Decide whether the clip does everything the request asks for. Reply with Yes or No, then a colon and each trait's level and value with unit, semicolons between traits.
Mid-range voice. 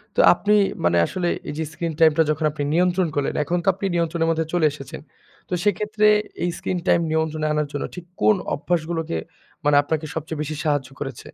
Yes: medium, 160 Hz